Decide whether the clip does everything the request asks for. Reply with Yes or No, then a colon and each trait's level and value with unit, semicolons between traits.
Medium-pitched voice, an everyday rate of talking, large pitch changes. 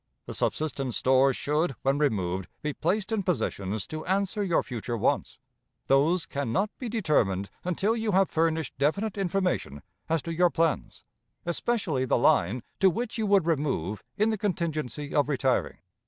Yes: medium, 155 Hz; average, 160 wpm; wide, 6.5 semitones